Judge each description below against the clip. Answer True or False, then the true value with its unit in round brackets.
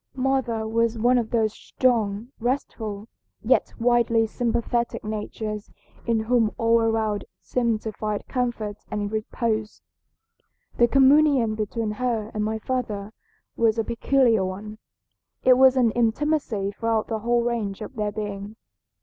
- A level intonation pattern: True (2.0 semitones)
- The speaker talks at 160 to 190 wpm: False (135 wpm)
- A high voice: True (225 Hz)